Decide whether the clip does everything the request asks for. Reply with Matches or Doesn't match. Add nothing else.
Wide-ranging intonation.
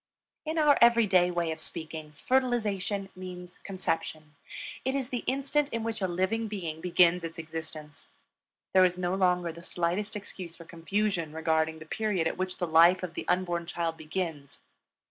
Doesn't match